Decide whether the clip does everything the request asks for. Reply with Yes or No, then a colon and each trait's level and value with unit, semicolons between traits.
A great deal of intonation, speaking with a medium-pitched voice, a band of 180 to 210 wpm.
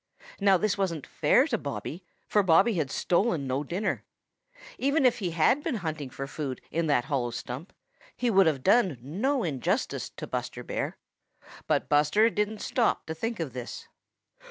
No: wide, 6.7 semitones; medium, 170 Hz; average, 170 wpm